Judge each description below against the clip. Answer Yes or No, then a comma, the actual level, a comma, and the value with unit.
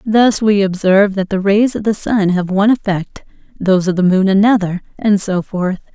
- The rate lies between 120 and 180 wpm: No, average, 200 wpm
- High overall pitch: Yes, high, 195 Hz